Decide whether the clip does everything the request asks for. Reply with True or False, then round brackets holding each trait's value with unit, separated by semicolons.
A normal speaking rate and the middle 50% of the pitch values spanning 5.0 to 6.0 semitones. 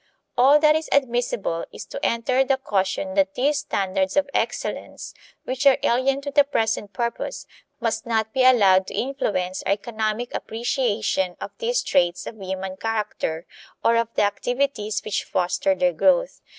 True (160 wpm; 5.5 semitones)